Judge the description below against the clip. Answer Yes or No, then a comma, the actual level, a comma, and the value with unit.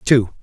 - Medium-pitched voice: No, low, 115 Hz